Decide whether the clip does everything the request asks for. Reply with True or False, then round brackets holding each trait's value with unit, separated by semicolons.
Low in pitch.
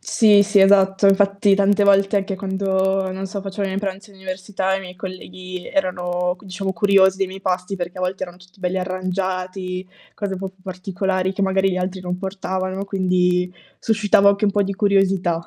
False (190 Hz)